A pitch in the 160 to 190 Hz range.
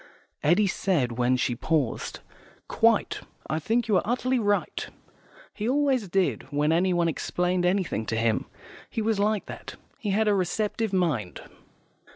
Yes: medium, 185 Hz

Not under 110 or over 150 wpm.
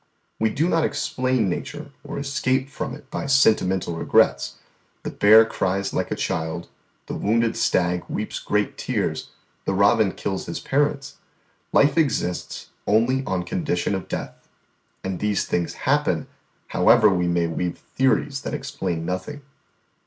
Yes: average, 145 wpm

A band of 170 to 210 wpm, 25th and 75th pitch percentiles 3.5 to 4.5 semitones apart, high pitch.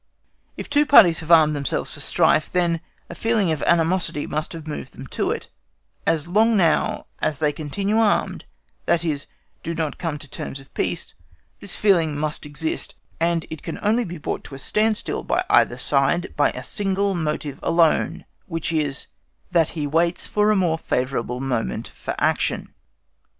No: average, 175 wpm; average, 3.8 semitones; medium, 165 Hz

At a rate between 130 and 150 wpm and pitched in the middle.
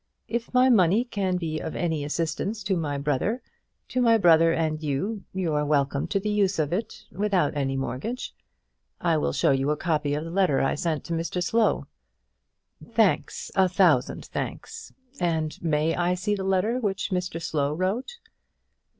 No: average, 175 wpm; medium, 175 Hz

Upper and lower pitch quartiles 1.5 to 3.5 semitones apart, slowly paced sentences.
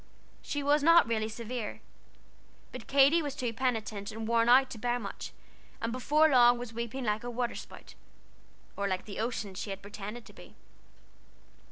No: average, 3.0 semitones; average, 175 wpm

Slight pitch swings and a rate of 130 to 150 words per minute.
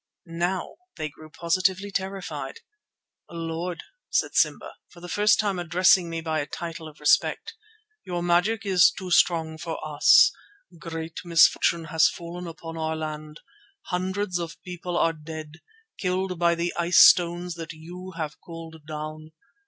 Yes: narrow, 2.0 semitones; average, 145 wpm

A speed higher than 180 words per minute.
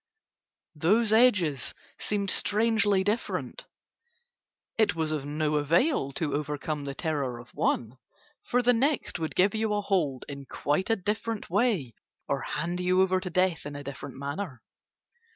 No: average, 150 wpm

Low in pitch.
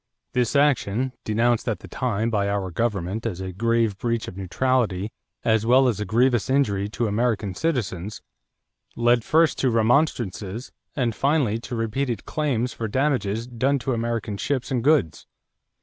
Yes: low, 115 Hz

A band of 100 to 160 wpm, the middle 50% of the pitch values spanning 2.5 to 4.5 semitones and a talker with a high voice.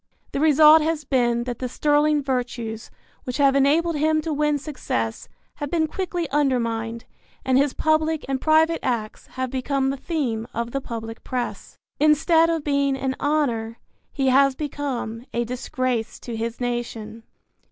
Yes: average, 155 wpm; average, 4.1 semitones; very high, 270 Hz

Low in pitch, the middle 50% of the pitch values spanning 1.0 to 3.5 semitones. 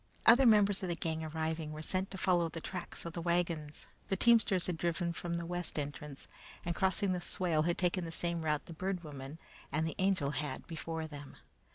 No: medium, 170 Hz; narrow, 2.6 semitones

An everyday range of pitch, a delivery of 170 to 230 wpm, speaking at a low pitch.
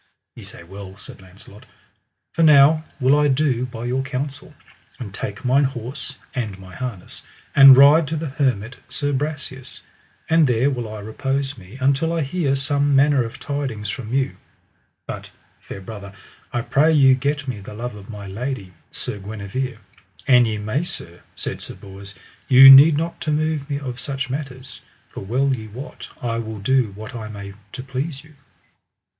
Yes: average, 4.6 semitones; average, 175 wpm; low, 130 Hz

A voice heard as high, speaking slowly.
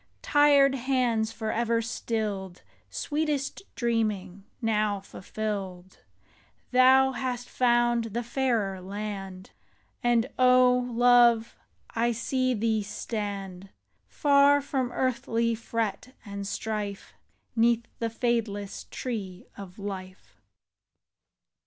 Yes: high, 230 Hz; slow, 90 wpm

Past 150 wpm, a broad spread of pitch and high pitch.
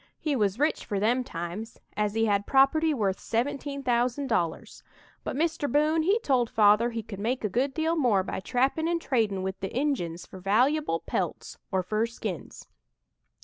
Yes: average, 180 wpm; wide, 5.8 semitones; high, 235 Hz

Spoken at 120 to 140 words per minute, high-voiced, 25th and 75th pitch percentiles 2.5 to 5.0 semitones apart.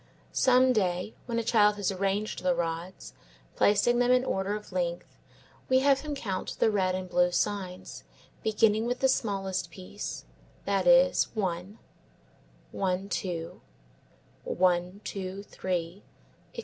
Yes: slow, 135 wpm; high, 195 Hz; average, 3.4 semitones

